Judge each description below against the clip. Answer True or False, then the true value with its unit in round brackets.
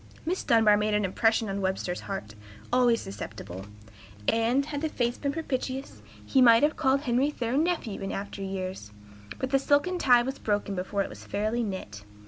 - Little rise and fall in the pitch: False (5.5 semitones)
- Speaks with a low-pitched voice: False (230 Hz)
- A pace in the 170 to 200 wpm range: True (180 wpm)